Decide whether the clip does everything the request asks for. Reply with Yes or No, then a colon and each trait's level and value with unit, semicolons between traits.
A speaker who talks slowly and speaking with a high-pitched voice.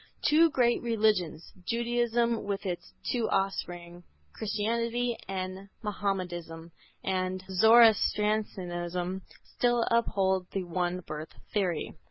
Yes: slow, 95 wpm; high, 195 Hz